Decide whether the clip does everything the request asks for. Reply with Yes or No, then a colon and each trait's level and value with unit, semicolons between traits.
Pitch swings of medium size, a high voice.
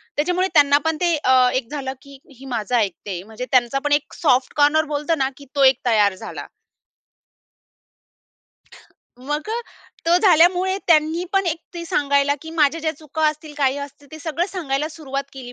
Yes: average, 3.3 semitones; very high, 290 Hz